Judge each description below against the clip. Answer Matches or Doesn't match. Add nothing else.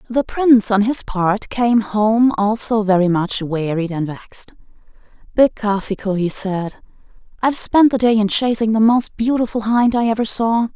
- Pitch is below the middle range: Doesn't match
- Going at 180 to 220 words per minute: Doesn't match